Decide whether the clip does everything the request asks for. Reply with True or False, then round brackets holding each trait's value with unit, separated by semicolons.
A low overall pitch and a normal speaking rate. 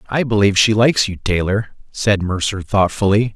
True (100 Hz; 160 wpm)